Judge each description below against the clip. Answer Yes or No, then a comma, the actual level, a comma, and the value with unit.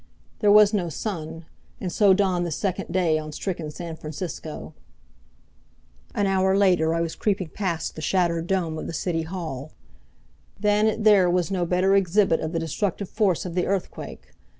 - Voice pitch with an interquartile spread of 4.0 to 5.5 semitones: No, average, 3.2 semitones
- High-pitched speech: No, medium, 180 Hz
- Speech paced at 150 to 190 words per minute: Yes, average, 175 wpm